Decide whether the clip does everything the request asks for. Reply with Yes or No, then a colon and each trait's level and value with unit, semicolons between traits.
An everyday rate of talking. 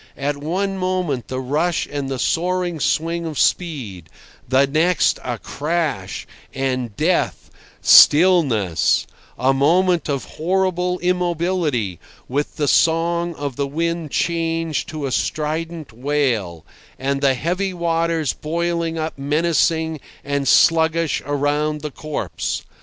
No: slow, 120 wpm